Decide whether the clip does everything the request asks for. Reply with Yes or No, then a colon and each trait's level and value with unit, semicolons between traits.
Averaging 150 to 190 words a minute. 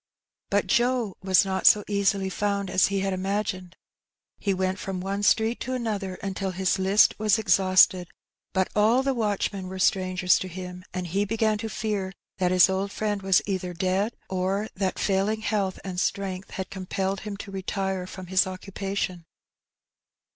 Yes: average, 170 wpm